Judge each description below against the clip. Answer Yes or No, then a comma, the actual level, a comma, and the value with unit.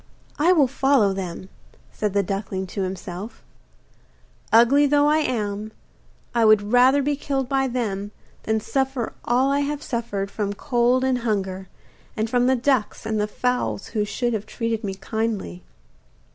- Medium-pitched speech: No, high, 230 Hz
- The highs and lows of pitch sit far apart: No, average, 4.5 semitones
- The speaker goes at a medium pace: Yes, average, 155 wpm